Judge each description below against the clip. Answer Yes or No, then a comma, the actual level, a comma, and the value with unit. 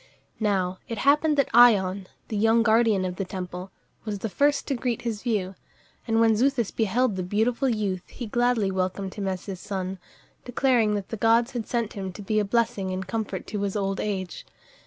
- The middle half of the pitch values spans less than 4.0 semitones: Yes, average, 3.6 semitones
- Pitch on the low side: No, high, 210 Hz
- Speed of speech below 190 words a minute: No, average, 200 wpm